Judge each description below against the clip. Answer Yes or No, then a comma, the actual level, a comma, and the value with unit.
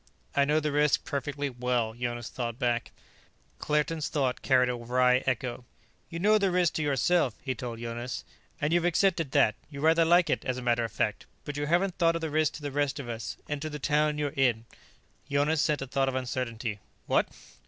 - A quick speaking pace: Yes, fast, 210 wpm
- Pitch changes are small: No, average, 3.9 semitones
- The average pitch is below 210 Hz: Yes, medium, 140 Hz